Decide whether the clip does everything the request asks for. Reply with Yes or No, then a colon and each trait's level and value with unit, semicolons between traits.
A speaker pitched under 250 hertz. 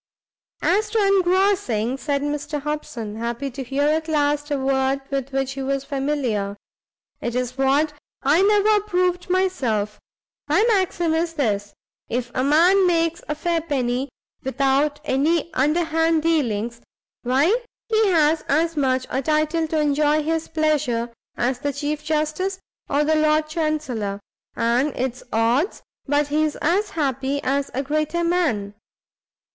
No: very high, 295 Hz